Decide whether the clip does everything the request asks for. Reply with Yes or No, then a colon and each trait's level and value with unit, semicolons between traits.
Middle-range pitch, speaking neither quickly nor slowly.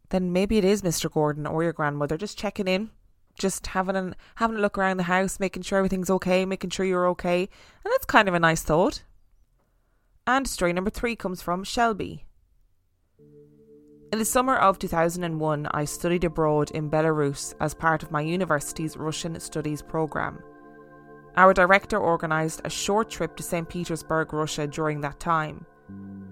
Yes: medium, 165 Hz; average, 170 wpm